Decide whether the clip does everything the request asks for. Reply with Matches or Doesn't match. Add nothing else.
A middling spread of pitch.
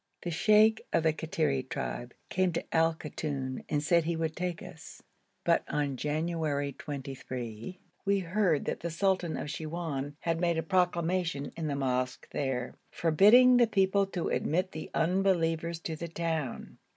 Matches